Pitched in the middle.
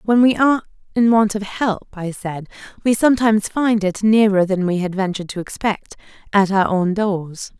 No: high, 205 Hz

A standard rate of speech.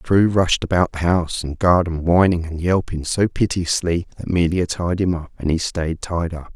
No: fast, 210 wpm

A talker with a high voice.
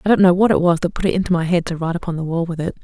No: medium, 175 Hz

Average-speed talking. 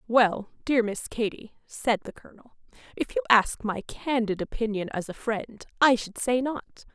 Yes: average, 175 wpm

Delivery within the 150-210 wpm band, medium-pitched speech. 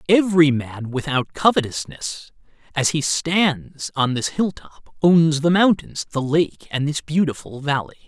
No: average, 140 wpm; medium, 150 Hz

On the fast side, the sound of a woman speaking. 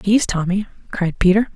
No: average, 155 wpm; female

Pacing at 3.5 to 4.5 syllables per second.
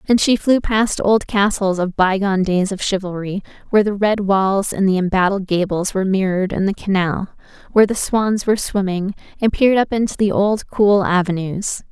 No: 5.2 syllables/s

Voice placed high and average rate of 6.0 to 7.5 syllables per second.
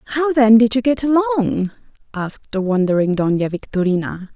Yes: high, 220 Hz; 6.3 syllables/s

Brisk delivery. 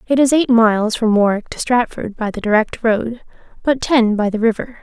Yes: fast, 210 wpm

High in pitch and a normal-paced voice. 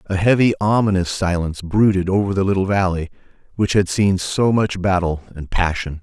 No: very low, 95 Hz; average, 170 wpm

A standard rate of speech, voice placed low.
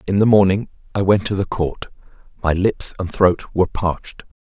Yes: average, 190 wpm; very low, 95 Hz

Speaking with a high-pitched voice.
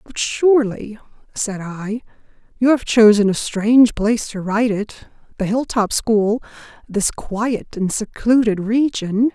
Yes: high, 220 Hz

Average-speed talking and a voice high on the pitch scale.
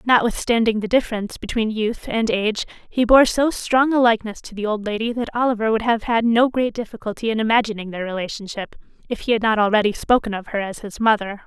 No: fast, 210 wpm; high, 220 Hz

